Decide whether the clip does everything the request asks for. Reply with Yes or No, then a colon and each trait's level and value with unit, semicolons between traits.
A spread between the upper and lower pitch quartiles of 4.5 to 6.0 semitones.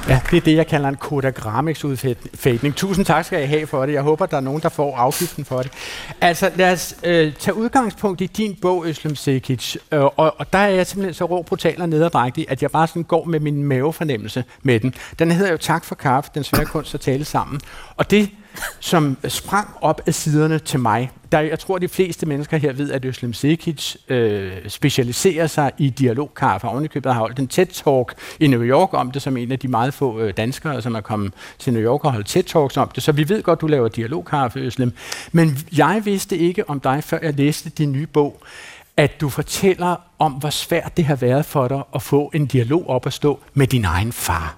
No: average, 4.0 semitones